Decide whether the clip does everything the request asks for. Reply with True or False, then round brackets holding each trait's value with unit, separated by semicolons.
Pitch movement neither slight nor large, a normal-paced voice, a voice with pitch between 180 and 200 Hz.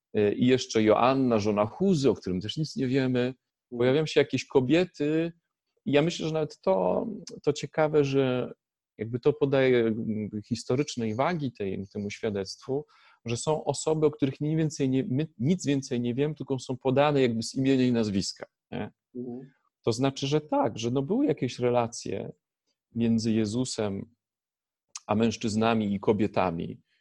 False (4.2 semitones; 150 wpm; 130 Hz)